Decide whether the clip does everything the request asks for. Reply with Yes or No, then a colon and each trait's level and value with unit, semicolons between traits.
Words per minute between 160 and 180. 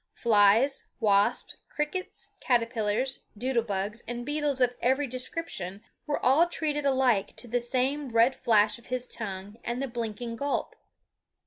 No: average, 140 wpm